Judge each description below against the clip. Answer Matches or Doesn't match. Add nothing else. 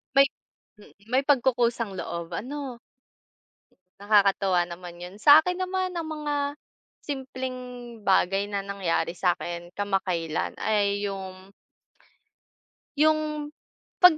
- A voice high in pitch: Matches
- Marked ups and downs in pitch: Matches